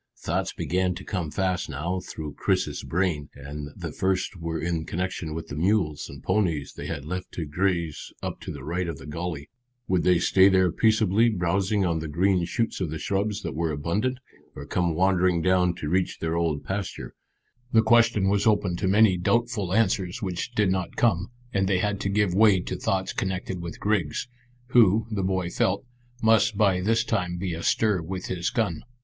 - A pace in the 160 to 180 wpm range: No, average, 190 wpm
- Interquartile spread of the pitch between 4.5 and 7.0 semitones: No, average, 3.0 semitones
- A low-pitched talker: Yes, very low, 95 Hz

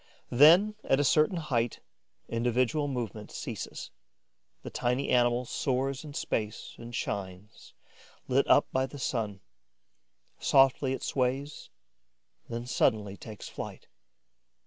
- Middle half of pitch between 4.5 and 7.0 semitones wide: No, average, 3.1 semitones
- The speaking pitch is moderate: No, low, 125 Hz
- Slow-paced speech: Yes, slow, 115 wpm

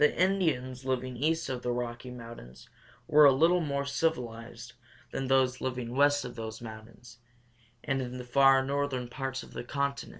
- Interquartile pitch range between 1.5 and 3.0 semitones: Yes, narrow, 2.5 semitones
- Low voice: Yes, low, 130 Hz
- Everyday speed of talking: Yes, average, 170 wpm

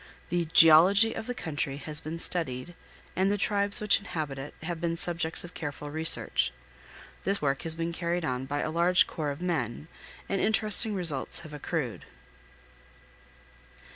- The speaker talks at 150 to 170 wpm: Yes, average, 160 wpm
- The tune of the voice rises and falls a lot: No, average, 3.4 semitones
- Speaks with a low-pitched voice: No, medium, 165 Hz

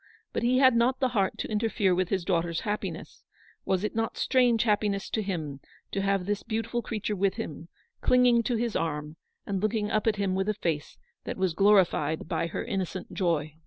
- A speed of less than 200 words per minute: No, fast, 205 wpm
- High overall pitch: Yes, high, 200 Hz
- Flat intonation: No, average, 3.8 semitones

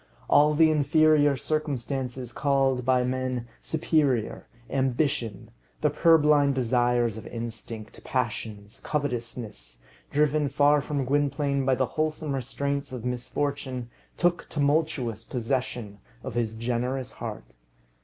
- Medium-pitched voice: No, low, 130 Hz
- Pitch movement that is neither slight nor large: Yes, average, 3.4 semitones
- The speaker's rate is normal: No, slow, 110 wpm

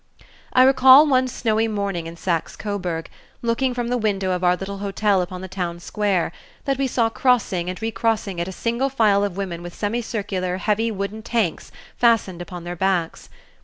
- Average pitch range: Yes, average, 4.1 semitones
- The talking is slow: No, average, 180 wpm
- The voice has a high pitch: Yes, high, 200 Hz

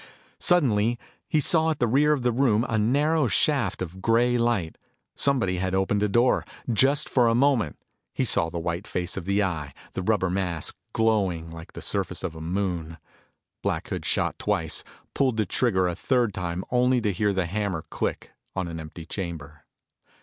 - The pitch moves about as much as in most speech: No, wide, 5.7 semitones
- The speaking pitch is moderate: No, low, 100 Hz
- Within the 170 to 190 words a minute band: Yes, average, 185 wpm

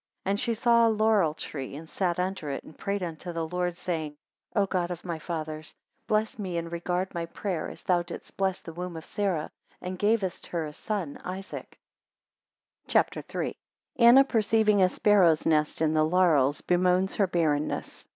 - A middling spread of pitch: Yes, average, 3.6 semitones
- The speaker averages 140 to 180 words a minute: No, average, 190 wpm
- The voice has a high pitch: No, medium, 180 Hz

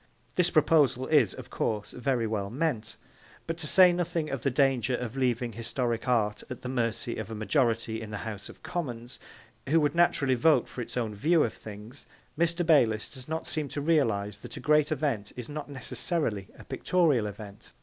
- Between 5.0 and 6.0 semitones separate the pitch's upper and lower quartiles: Yes, average, 5.3 semitones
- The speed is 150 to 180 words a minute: No, average, 190 wpm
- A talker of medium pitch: No, low, 125 Hz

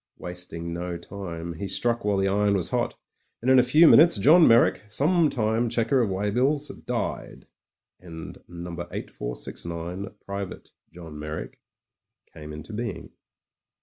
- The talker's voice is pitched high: No, low, 100 Hz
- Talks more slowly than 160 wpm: Yes, average, 140 wpm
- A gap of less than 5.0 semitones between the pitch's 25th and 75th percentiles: No, wide, 5.6 semitones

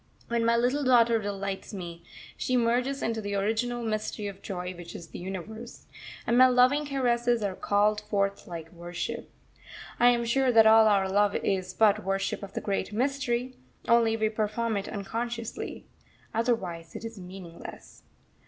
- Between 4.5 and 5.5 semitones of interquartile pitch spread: No, average, 3.4 semitones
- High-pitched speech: Yes, high, 220 Hz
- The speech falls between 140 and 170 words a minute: Yes, average, 160 wpm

